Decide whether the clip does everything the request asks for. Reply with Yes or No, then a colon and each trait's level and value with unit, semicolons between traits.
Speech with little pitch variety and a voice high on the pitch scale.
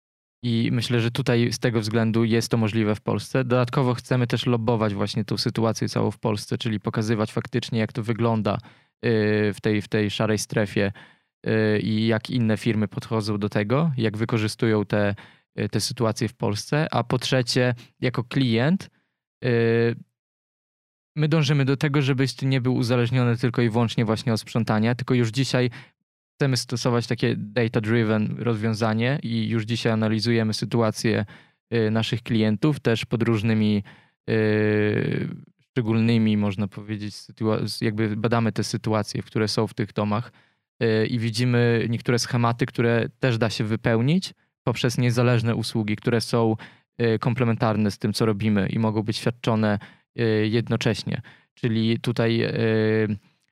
No: narrow, 2.1 semitones; low, 115 Hz